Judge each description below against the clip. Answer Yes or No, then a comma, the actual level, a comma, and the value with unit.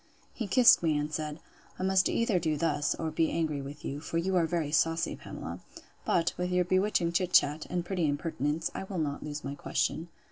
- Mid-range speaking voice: Yes, medium, 165 Hz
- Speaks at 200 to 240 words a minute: Yes, fast, 205 wpm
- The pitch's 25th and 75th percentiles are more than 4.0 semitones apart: No, average, 3.1 semitones